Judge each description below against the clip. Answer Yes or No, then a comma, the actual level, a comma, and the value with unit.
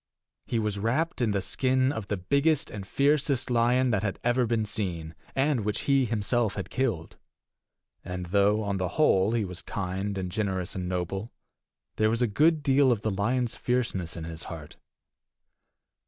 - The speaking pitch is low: Yes, low, 110 Hz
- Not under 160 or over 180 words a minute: Yes, average, 175 wpm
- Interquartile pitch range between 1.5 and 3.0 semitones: No, average, 4.8 semitones